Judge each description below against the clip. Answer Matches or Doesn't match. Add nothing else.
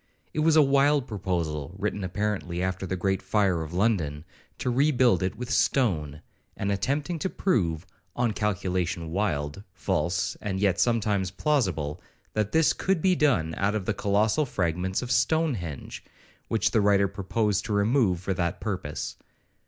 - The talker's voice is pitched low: Matches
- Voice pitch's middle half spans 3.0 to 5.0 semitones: Doesn't match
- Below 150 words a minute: Doesn't match